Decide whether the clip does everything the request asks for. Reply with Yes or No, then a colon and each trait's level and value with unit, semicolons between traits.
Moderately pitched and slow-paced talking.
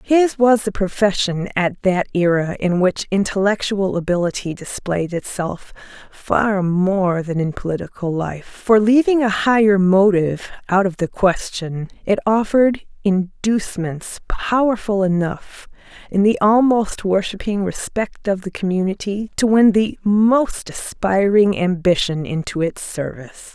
No: high, 195 Hz; slow, 125 wpm